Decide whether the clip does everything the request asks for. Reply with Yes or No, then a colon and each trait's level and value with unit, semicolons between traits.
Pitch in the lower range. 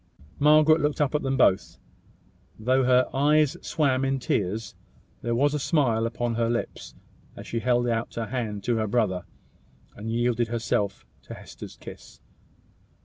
Yes: low, 120 Hz